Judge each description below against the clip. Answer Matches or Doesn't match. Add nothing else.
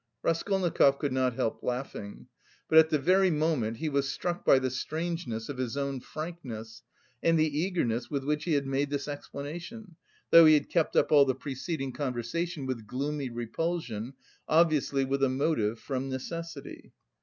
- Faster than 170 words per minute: Doesn't match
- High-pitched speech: Doesn't match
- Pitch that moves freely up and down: Doesn't match